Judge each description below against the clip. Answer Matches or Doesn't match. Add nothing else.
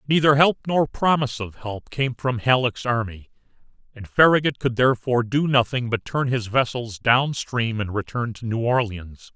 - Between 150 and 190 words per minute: Matches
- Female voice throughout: Doesn't match